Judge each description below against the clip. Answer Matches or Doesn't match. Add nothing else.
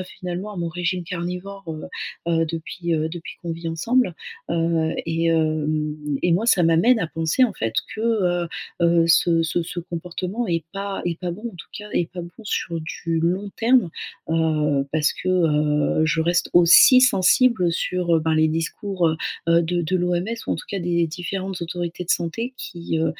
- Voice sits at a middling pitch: Matches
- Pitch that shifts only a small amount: Matches